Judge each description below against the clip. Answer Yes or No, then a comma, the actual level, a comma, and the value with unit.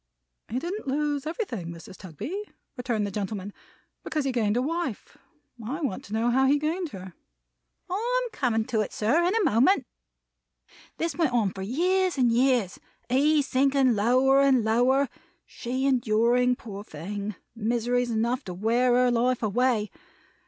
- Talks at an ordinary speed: Yes, average, 160 wpm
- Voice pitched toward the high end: Yes, high, 245 Hz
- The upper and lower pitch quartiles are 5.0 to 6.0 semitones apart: No, average, 4.3 semitones